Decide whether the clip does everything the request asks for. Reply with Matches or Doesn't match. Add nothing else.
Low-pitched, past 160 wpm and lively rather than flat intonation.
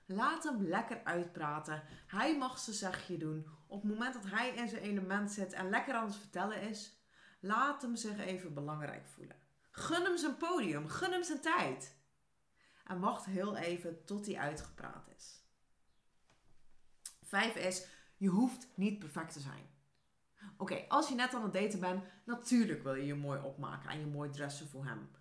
Doesn't match